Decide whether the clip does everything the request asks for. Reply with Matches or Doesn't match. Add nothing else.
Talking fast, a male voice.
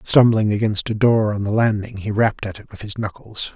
Matches